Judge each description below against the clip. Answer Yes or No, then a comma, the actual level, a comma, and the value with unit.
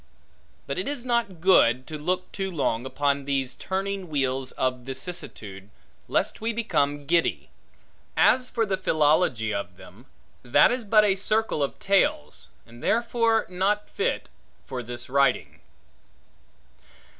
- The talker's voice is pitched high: No, medium, 160 Hz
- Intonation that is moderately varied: No, wide, 8.1 semitones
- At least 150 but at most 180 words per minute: No, slow, 135 wpm